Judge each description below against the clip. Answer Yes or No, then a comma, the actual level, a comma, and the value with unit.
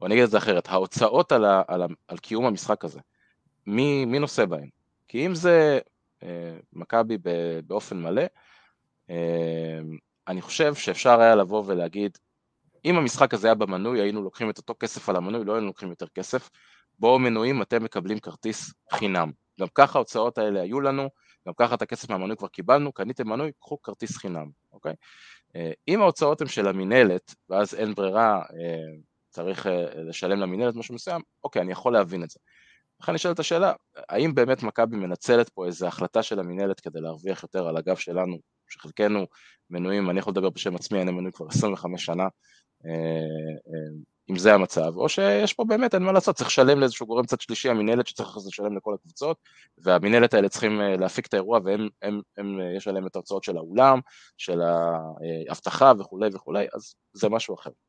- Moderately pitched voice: No, low, 100 Hz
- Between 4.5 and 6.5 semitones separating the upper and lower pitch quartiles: Yes, wide, 5.4 semitones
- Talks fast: Yes, fast, 175 wpm